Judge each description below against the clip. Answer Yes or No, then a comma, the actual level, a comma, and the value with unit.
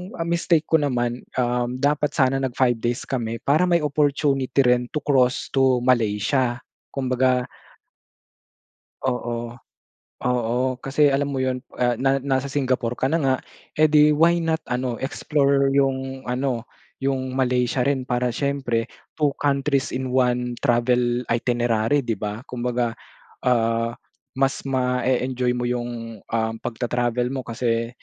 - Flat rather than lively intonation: Yes, narrow, 2.2 semitones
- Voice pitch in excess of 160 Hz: No, low, 130 Hz